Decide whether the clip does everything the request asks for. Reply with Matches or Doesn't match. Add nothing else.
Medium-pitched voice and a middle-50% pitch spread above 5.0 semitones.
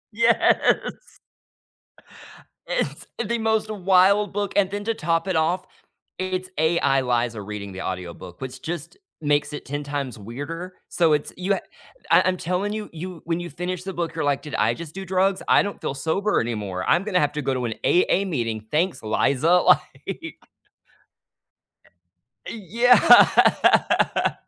Matches